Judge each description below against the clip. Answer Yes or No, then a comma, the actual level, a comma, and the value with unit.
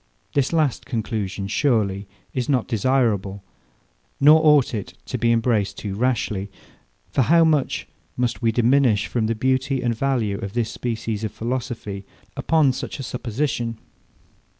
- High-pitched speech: No, low, 120 Hz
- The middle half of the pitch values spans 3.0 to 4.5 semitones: Yes, average, 3.7 semitones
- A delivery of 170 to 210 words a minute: No, average, 145 wpm